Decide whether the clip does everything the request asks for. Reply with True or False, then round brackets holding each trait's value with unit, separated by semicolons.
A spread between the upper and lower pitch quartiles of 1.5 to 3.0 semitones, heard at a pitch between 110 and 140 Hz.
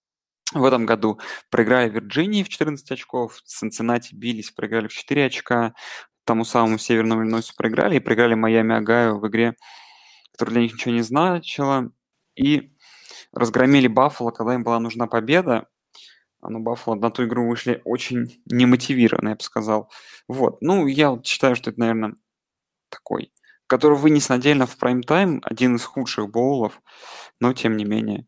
True (2.5 semitones; 120 Hz)